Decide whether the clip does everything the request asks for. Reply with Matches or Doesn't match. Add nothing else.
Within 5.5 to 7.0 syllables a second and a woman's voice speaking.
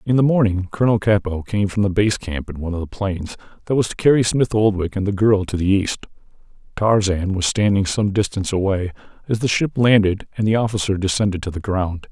Doesn't match